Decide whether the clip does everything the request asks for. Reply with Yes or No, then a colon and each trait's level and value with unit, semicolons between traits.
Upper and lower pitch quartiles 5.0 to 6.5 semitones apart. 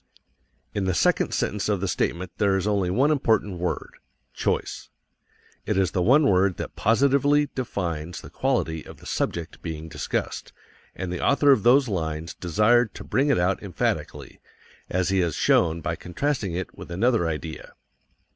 Yes: wide, 5.6 semitones